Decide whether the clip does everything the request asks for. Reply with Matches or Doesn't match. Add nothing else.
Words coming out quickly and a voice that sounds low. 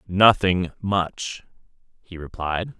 Doesn't match